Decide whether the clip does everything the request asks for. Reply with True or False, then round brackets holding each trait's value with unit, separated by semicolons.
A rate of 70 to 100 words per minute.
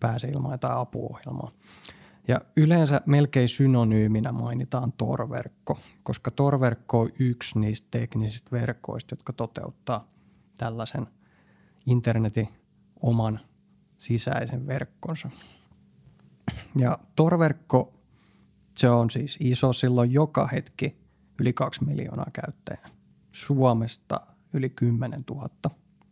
True (95 wpm)